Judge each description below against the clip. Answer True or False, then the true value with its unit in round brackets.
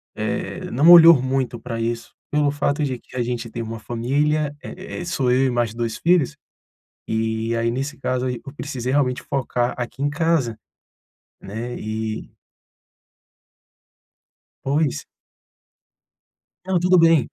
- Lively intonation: False (4.0 semitones)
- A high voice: False (130 Hz)